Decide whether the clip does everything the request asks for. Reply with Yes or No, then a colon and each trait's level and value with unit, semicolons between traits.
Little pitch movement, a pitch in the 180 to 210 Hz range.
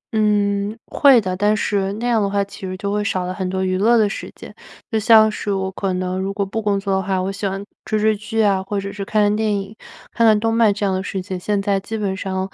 Yes: narrow, 1.9 semitones; high, 200 Hz